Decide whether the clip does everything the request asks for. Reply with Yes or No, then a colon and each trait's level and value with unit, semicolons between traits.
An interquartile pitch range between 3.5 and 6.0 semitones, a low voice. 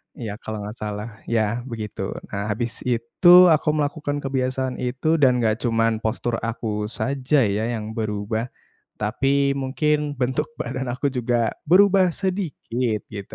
Yes: average, 4.2 semitones; low, 125 Hz